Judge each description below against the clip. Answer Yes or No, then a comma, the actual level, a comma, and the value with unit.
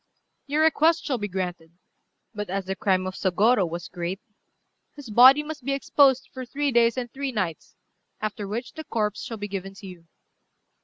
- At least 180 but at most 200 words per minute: Yes, average, 185 wpm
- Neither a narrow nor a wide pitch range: No, wide, 6.0 semitones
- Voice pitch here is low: No, high, 215 Hz